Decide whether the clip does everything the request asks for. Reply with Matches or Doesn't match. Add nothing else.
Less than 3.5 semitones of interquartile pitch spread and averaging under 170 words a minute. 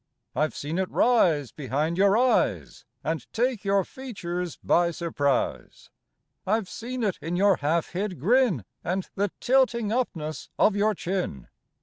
Doesn't match